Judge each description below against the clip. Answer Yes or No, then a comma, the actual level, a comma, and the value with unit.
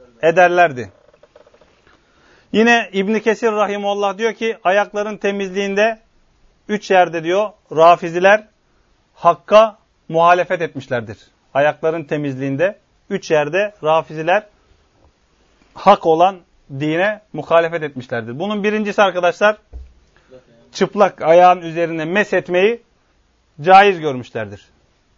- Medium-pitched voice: Yes, medium, 180 Hz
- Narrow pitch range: No, average, 5.3 semitones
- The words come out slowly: Yes, slow, 85 wpm